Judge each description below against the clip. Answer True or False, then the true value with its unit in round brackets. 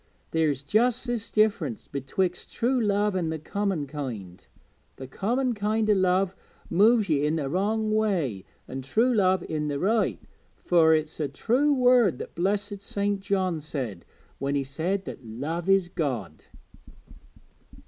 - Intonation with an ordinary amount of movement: False (6.2 semitones)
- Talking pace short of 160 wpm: True (150 wpm)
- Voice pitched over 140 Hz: True (185 Hz)